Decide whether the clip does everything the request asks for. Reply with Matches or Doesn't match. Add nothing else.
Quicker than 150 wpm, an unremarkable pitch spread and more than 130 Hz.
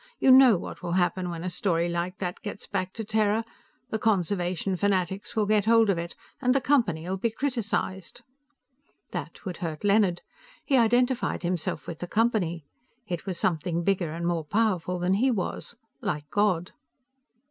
Matches